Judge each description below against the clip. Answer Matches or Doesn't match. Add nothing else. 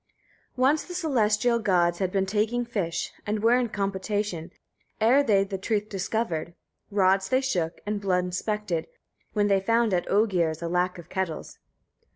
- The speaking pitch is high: Matches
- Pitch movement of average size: Matches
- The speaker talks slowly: Doesn't match